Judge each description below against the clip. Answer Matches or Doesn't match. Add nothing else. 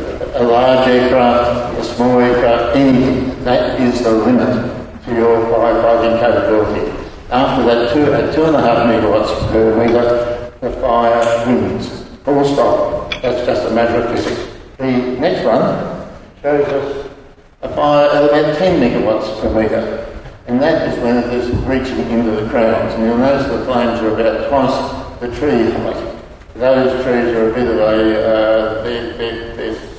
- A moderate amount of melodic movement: Doesn't match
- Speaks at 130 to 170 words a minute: Matches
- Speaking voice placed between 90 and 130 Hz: Matches